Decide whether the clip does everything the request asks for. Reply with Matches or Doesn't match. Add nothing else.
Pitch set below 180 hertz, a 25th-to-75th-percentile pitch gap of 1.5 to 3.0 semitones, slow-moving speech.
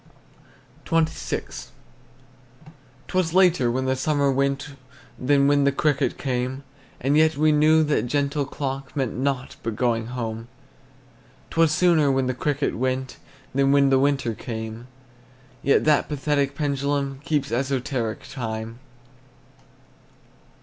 Matches